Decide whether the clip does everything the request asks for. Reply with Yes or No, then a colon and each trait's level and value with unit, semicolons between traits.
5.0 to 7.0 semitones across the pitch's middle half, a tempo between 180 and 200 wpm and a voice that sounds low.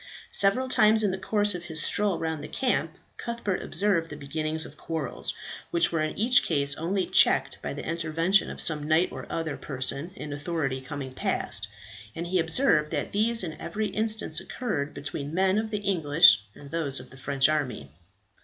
No: average, 5.3 semitones; average, 185 wpm; medium, 165 Hz